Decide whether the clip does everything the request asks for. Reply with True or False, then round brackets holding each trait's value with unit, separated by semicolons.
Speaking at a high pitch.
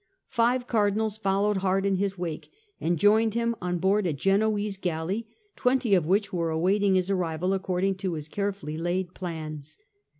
True (195 Hz)